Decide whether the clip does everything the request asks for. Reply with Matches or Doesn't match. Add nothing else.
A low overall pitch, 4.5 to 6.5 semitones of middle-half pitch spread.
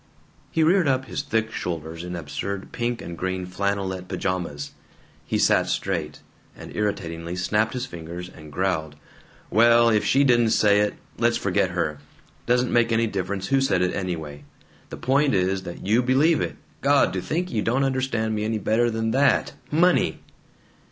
Matches